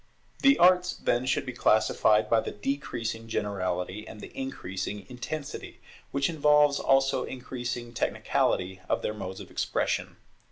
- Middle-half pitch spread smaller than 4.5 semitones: No, average, 4.9 semitones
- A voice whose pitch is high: No, low, 120 Hz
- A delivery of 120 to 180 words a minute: Yes, slow, 135 wpm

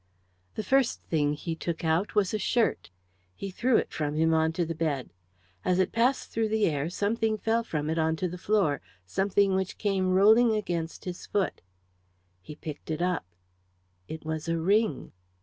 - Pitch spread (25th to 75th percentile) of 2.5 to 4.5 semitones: No, average, 4.9 semitones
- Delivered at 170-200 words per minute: Yes, average, 185 wpm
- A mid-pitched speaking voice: Yes, medium, 180 Hz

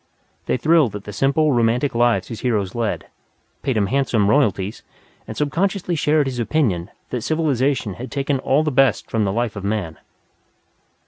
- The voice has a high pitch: No, low, 125 Hz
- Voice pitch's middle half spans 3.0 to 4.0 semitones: No, average, 5.2 semitones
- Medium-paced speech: Yes, average, 170 wpm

